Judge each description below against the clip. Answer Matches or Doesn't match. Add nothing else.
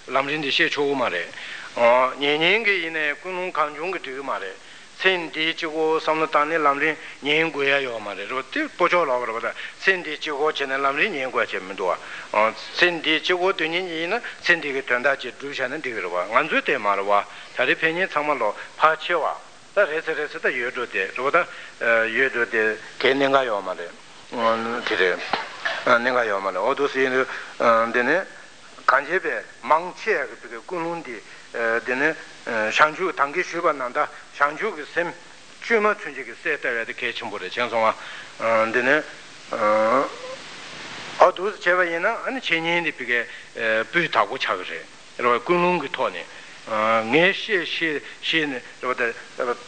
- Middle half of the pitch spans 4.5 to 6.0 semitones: Matches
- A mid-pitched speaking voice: Matches